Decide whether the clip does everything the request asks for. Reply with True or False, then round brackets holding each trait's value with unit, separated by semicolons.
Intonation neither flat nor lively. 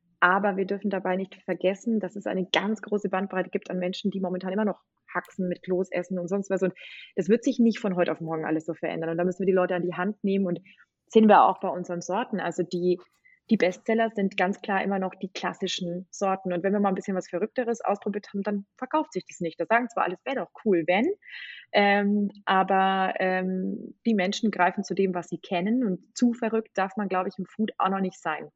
False (2.3 semitones)